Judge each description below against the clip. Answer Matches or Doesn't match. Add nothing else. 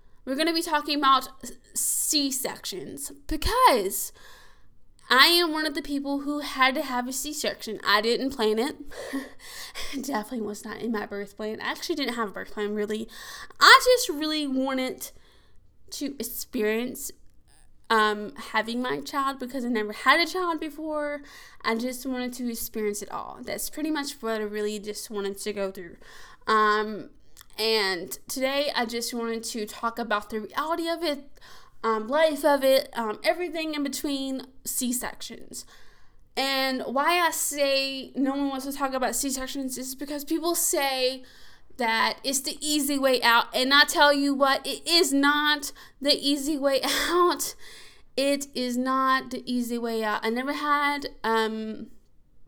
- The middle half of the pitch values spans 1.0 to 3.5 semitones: Doesn't match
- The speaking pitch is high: Matches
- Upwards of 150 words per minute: Matches